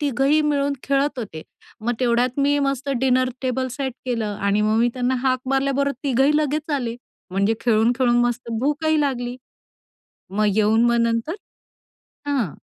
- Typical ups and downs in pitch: Yes, average, 3.1 semitones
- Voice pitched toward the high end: Yes, very high, 255 Hz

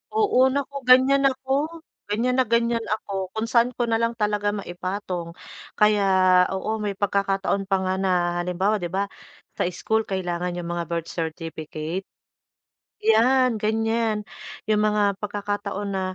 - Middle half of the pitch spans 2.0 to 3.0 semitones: No, average, 3.5 semitones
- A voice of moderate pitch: No, high, 205 Hz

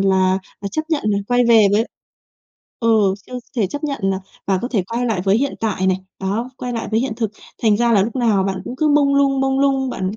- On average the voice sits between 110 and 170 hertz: No, high, 225 Hz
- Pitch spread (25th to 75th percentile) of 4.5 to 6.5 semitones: Yes, average, 5.2 semitones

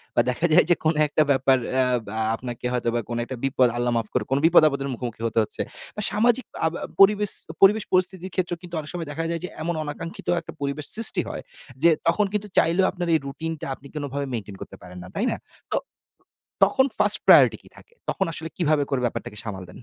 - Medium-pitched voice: Yes, medium, 155 Hz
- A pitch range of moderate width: No, wide, 5.9 semitones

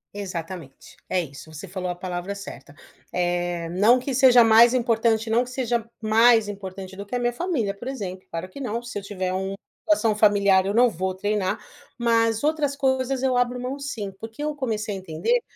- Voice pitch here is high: Yes, high, 215 Hz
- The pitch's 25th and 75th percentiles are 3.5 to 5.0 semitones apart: Yes, average, 4.6 semitones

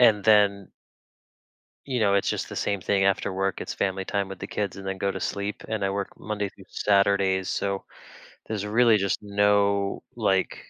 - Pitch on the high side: No, low, 100 Hz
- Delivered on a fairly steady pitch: Yes, narrow, 1.1 semitones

